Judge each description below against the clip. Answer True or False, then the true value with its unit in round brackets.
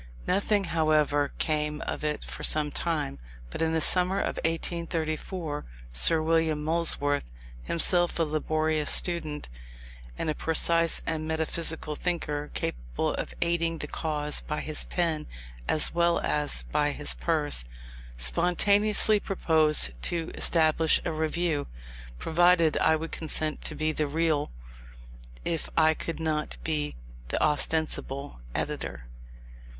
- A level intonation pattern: True (1.8 semitones)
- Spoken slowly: True (125 wpm)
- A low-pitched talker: False (155 Hz)